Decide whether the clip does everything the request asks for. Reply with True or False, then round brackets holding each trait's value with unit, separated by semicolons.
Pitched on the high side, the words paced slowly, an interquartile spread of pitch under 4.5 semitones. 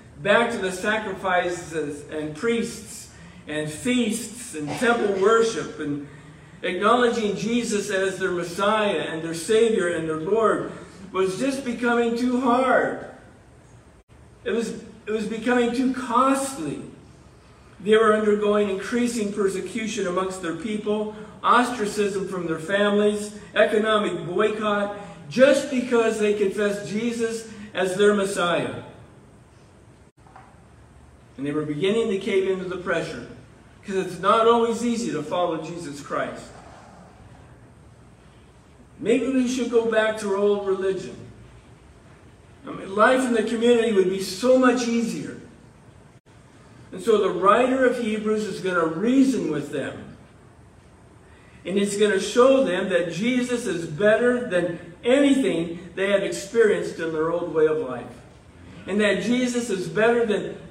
True (210 Hz; 130 wpm; 4.1 semitones)